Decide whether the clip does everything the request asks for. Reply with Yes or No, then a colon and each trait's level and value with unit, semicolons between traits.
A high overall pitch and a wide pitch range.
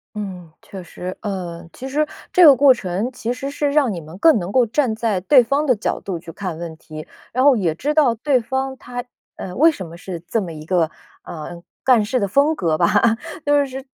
Yes: high, 220 Hz; wide, 7.1 semitones